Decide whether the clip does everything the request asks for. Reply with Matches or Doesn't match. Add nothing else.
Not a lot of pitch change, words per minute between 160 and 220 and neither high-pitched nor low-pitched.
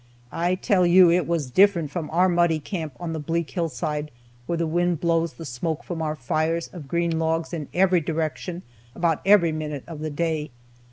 Matches